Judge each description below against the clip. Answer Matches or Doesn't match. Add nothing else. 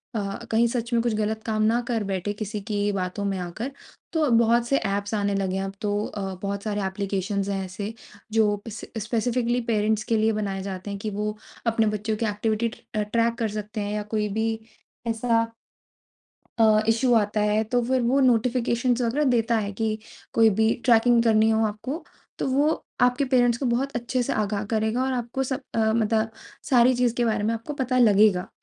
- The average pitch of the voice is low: Doesn't match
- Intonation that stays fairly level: Matches